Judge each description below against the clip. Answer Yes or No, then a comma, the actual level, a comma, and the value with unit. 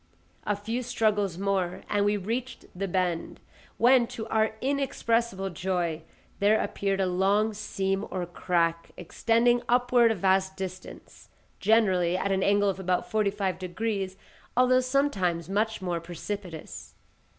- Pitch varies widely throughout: No, average, 3.3 semitones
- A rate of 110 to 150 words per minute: Yes, average, 140 wpm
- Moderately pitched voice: No, high, 195 Hz